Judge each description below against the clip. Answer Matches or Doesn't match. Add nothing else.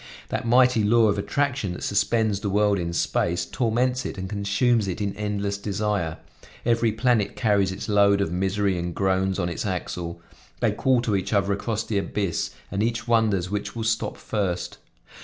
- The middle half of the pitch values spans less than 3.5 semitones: Matches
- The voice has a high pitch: Doesn't match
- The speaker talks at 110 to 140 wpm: Doesn't match